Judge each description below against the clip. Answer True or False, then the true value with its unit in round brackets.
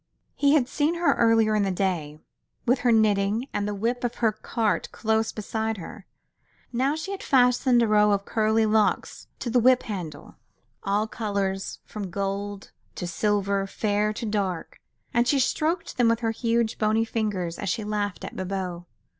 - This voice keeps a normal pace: True (175 wpm)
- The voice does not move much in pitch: False (3.0 semitones)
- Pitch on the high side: True (215 Hz)